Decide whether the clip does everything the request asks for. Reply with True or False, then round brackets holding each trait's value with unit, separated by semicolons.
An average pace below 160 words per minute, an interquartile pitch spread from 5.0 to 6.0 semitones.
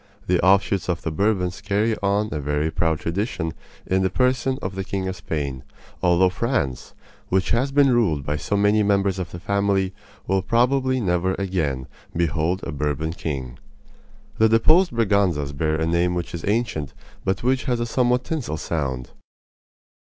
False (165 wpm; 5.3 semitones)